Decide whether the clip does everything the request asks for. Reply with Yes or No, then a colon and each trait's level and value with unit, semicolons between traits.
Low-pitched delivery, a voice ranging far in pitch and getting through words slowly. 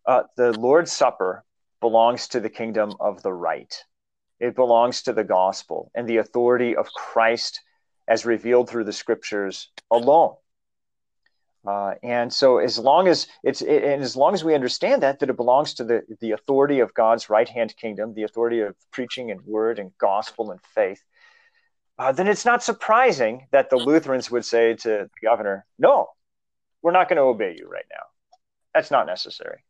No: low, 120 Hz; wide, 5.7 semitones; average, 180 wpm